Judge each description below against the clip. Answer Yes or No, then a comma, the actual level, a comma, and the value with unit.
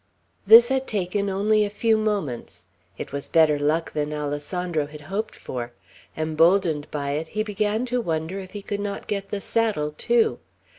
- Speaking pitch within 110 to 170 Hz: No, medium, 185 Hz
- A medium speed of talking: Yes, average, 170 wpm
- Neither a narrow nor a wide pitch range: No, wide, 5.9 semitones